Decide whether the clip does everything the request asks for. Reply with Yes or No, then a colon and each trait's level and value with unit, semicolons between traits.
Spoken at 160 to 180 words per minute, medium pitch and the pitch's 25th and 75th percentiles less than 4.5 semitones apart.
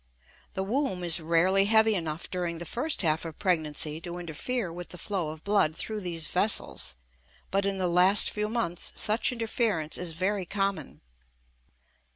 Yes: average, 165 wpm; medium, 180 Hz; average, 3.9 semitones